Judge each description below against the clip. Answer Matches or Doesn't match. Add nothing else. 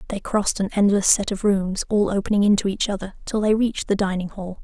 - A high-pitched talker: Matches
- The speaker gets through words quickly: Matches